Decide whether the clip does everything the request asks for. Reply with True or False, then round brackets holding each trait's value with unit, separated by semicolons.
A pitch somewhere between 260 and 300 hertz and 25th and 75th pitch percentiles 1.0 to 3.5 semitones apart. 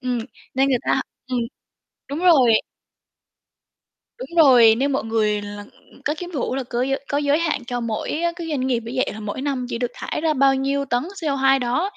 True (265 Hz; 3.2 semitones)